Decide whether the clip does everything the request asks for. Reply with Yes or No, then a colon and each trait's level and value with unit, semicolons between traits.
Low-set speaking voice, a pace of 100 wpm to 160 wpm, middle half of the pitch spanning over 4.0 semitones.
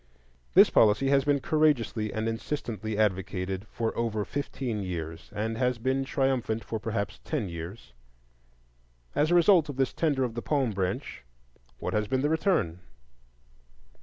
Yes: low, 115 Hz; average, 150 wpm; average, 4.7 semitones